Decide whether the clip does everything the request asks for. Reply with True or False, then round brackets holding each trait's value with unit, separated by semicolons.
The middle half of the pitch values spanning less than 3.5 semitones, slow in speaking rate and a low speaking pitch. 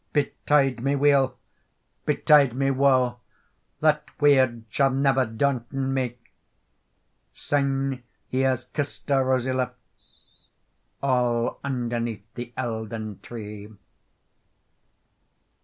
True (2.4 semitones; 90 wpm; 130 Hz)